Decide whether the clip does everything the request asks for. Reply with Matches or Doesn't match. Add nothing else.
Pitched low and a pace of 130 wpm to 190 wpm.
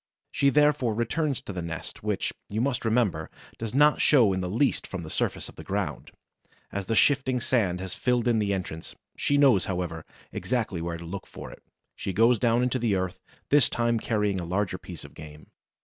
Doesn't match